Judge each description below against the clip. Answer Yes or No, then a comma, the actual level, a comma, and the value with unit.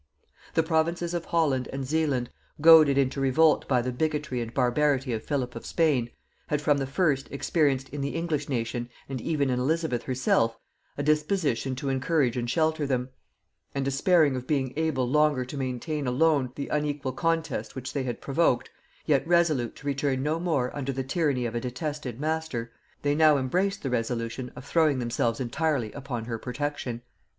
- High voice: No, medium, 140 Hz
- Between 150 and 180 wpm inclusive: Yes, average, 175 wpm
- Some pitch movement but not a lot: Yes, average, 3.5 semitones